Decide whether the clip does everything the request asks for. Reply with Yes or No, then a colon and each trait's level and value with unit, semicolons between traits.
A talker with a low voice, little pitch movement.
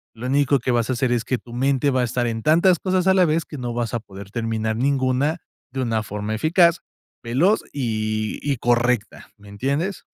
No: low, 125 Hz; average, 4.2 semitones